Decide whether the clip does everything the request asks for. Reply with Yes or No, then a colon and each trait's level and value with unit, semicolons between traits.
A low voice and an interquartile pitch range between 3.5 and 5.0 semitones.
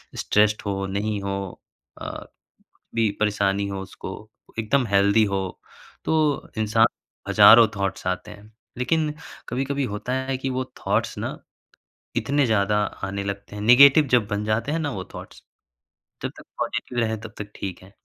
Yes: low, 105 Hz; average, 4.0 semitones